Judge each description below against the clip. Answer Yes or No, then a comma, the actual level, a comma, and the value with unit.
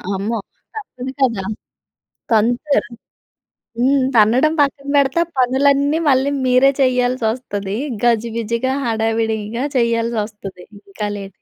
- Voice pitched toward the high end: Yes, high, 240 Hz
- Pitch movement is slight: No, average, 3.2 semitones